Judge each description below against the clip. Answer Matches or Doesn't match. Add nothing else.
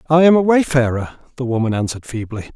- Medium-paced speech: Matches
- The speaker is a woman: Doesn't match